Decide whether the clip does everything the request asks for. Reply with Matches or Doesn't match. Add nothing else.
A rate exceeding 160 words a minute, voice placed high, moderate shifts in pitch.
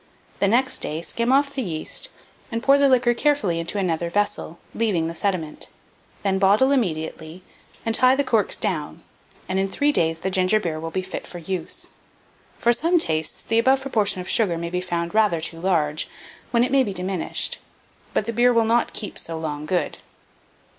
Doesn't match